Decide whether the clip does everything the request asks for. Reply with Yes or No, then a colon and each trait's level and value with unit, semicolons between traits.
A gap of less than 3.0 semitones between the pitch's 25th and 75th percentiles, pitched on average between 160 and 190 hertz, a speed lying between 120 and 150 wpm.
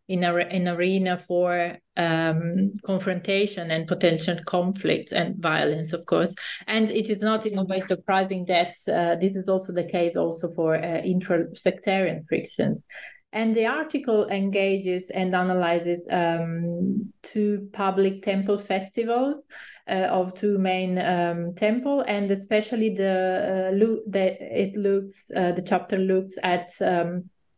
Yes: narrow, 2.4 semitones; medium, 185 Hz; average, 145 wpm